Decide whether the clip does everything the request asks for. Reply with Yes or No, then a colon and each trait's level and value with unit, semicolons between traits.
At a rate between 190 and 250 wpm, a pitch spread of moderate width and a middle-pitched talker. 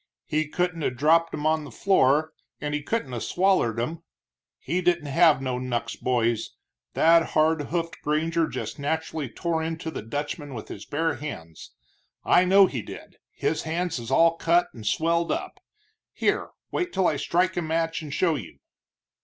No: average, 175 wpm; average, 3.6 semitones; medium, 160 Hz